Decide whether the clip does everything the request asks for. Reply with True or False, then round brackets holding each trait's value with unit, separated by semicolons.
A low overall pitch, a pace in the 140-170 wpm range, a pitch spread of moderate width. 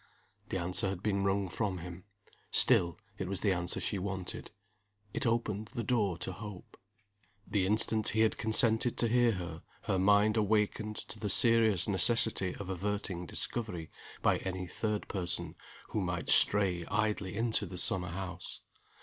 True (100 Hz; 160 wpm; 3.1 semitones)